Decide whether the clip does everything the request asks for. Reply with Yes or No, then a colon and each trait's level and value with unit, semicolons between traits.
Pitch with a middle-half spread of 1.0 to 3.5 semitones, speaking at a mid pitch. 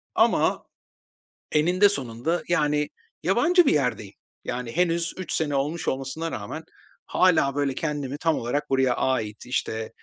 No: average, 4.3 semitones; medium, 145 Hz